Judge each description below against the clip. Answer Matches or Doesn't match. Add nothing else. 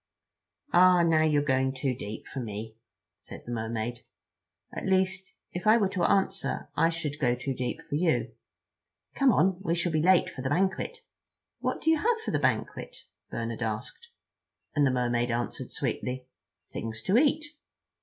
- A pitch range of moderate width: Doesn't match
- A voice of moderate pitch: Matches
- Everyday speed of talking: Matches